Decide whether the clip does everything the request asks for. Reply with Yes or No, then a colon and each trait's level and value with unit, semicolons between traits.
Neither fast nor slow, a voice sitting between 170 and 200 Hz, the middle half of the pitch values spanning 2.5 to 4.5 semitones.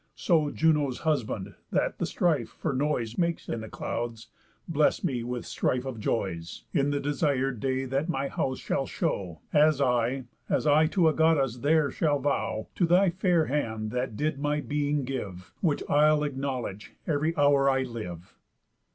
No: average, 170 wpm; medium, 140 Hz; average, 4.1 semitones